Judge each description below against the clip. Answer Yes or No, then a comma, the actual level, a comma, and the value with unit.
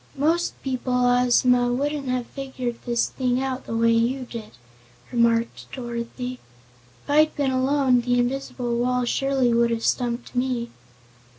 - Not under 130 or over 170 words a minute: Yes, average, 140 wpm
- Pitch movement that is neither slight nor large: No, narrow, 1.9 semitones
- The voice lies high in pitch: Yes, very high, 250 Hz